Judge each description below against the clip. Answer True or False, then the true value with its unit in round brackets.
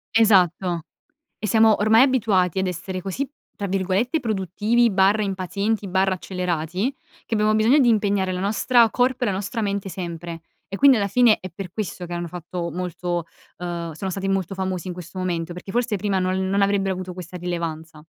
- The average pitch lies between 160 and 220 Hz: True (190 Hz)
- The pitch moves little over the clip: False (3.0 semitones)